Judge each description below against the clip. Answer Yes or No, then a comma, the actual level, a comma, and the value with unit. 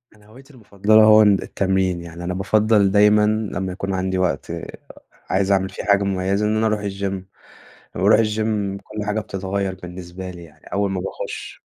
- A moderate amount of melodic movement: No, narrow, 2.1 semitones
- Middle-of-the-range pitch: No, low, 100 Hz